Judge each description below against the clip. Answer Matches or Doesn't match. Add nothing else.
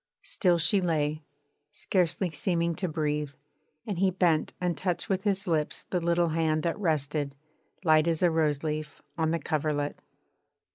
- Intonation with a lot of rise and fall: Doesn't match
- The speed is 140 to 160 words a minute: Matches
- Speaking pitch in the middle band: Matches